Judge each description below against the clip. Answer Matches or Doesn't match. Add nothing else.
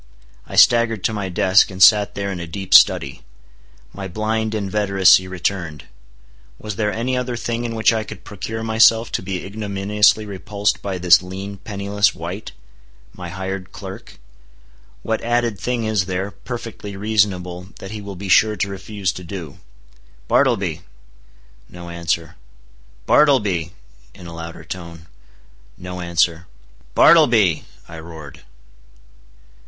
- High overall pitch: Doesn't match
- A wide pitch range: Doesn't match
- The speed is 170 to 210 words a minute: Doesn't match